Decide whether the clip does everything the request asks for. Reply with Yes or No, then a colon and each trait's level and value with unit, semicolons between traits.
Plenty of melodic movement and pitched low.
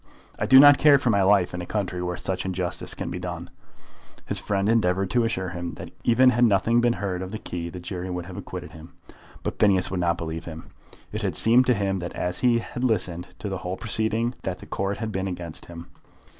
No: average, 4.1 semitones; very low, 95 Hz